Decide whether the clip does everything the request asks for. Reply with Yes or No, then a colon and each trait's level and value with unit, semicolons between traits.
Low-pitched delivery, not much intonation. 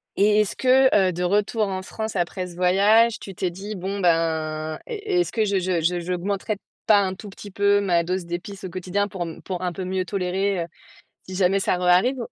No: high, 190 Hz; narrow, 2.3 semitones